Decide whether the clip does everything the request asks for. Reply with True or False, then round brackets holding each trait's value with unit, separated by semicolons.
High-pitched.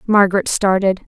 True (195 Hz)